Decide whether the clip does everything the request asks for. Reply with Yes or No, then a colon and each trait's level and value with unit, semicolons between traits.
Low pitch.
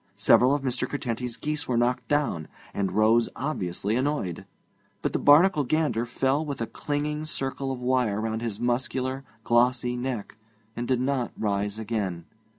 Yes: low, 125 Hz